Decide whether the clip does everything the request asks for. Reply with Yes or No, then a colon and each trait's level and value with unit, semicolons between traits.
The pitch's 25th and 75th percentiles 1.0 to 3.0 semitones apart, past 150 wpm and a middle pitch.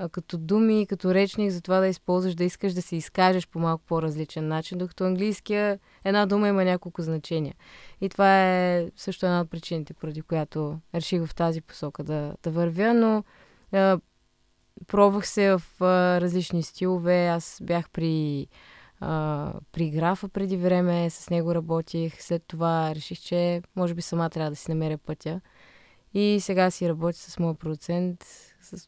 Yes: narrow, 2.4 semitones; average, 160 wpm; medium, 175 Hz